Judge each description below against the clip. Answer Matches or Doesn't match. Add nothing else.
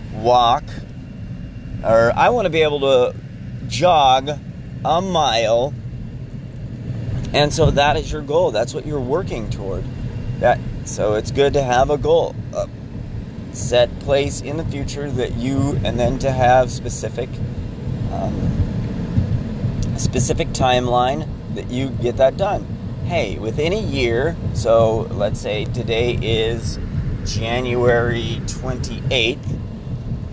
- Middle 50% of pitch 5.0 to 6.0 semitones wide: Doesn't match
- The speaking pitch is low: Matches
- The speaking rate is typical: Doesn't match